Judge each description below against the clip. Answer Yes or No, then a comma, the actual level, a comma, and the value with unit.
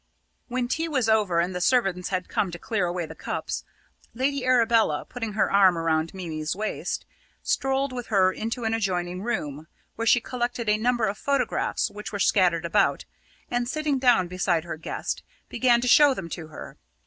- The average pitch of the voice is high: Yes, high, 210 Hz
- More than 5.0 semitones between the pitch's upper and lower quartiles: Yes, wide, 5.6 semitones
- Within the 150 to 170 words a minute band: No, average, 185 wpm